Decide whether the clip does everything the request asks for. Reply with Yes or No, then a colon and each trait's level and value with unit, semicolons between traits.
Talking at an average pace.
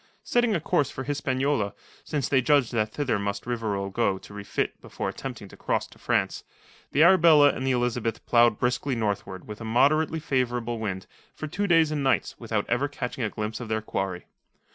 Yes: average, 190 wpm